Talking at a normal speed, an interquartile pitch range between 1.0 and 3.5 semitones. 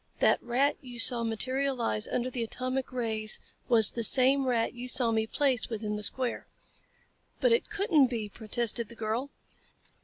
Yes: average, 160 wpm; average, 2.7 semitones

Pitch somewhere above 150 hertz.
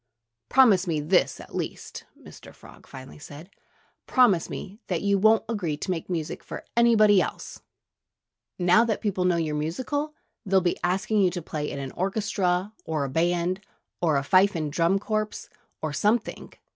Yes: medium, 185 Hz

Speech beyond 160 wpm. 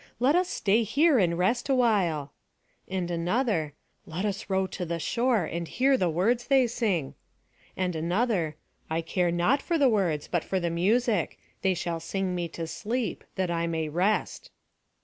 Yes: average, 170 wpm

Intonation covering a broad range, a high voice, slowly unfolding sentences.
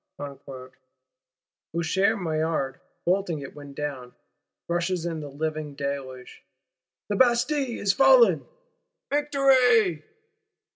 No: wide, 7.3 semitones; medium, 160 Hz; slow, 100 wpm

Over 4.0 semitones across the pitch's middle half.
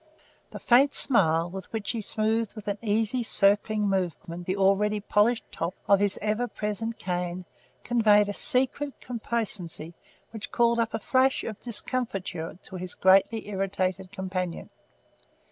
No: average, 3.3 semitones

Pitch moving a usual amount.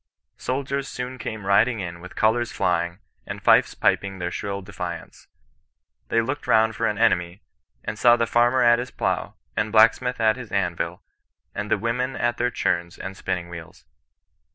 Yes: average, 4.6 semitones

